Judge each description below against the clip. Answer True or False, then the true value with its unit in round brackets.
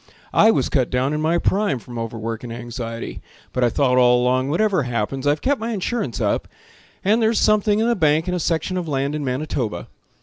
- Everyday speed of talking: False (210 wpm)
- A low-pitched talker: False (145 Hz)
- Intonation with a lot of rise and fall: True (7.3 semitones)